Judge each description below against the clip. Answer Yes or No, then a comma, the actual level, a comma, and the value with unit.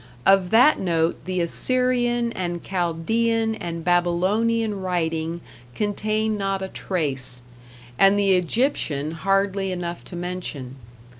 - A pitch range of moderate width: Yes, average, 4.0 semitones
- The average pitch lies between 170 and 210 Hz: Yes, medium, 185 Hz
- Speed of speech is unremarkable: No, slow, 115 wpm